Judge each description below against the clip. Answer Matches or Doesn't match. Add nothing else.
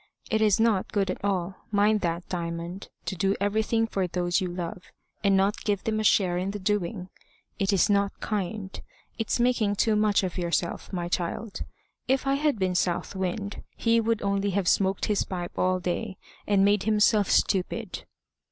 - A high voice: Matches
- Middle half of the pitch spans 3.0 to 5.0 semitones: Doesn't match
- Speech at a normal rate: Matches